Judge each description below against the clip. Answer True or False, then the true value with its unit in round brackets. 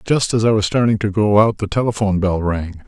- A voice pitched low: True (105 Hz)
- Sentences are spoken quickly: True (250 wpm)